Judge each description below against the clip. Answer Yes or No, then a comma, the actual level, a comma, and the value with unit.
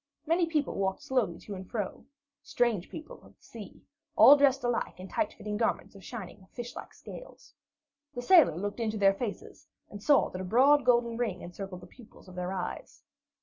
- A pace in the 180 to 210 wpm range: Yes, average, 190 wpm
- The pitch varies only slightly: No, average, 5.0 semitones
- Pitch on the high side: Yes, high, 220 Hz